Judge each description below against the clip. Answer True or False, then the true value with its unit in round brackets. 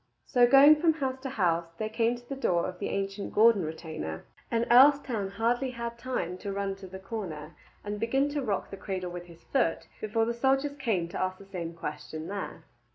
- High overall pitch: True (210 Hz)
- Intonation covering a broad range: True (5.7 semitones)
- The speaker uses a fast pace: True (210 wpm)